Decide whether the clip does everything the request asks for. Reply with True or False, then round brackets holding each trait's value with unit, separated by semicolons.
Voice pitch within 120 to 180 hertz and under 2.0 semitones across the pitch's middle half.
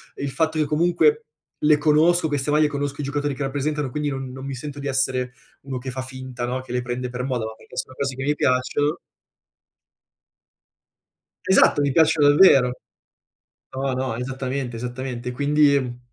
False (135 Hz; 2.6 semitones)